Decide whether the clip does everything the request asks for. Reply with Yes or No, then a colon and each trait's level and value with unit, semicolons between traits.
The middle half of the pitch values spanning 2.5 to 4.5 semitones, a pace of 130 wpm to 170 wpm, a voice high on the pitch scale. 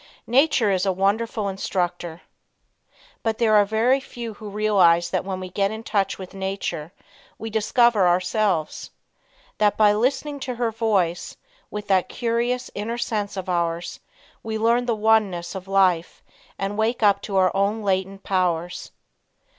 Yes: average, 3.1 semitones; average, 155 wpm; high, 205 Hz